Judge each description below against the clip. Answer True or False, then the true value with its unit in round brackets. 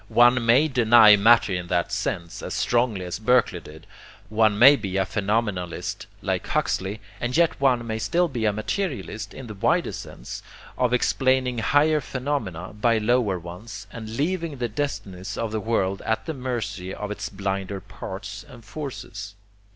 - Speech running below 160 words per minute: False (165 wpm)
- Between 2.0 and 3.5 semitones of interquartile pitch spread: False (4.3 semitones)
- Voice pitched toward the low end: True (110 Hz)